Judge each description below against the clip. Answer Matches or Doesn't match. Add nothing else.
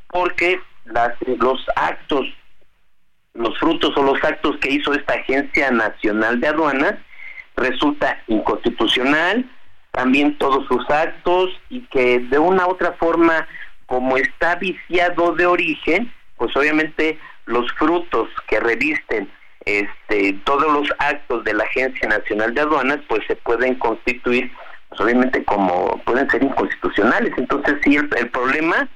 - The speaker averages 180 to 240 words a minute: Doesn't match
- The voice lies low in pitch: Doesn't match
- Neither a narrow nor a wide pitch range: Doesn't match